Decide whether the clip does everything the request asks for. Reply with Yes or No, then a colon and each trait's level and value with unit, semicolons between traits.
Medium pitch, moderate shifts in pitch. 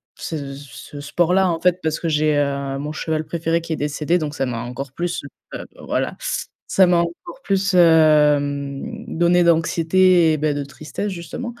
Yes: medium, 160 Hz; average, 3.3 semitones